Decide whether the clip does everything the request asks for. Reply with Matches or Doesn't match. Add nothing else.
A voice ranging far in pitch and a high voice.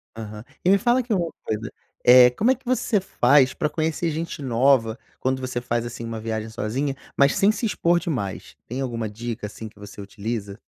Doesn't match